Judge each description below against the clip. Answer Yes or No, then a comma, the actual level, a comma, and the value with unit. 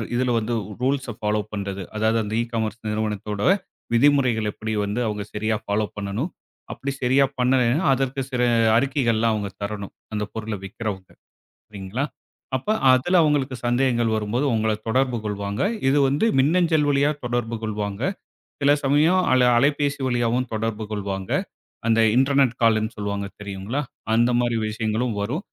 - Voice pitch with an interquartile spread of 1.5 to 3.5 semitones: No, average, 4.0 semitones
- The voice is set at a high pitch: No, low, 115 Hz